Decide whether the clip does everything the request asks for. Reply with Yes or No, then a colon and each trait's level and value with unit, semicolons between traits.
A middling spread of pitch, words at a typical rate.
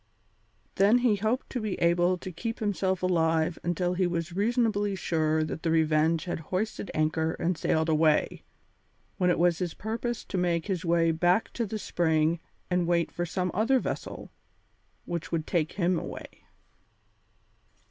Yes: average, 3.4 semitones; average, 160 wpm